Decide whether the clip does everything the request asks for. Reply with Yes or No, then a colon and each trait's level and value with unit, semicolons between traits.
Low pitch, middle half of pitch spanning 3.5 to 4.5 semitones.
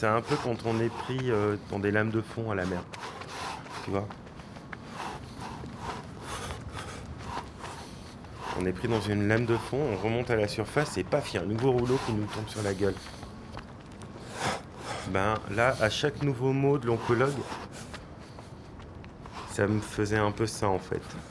No: low, 110 Hz; average, 3.0 semitones